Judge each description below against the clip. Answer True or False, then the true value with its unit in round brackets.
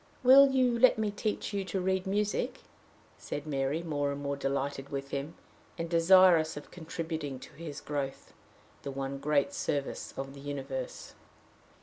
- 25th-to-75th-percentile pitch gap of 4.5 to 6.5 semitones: True (5.2 semitones)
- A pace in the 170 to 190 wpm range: False (155 wpm)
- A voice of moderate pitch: True (150 Hz)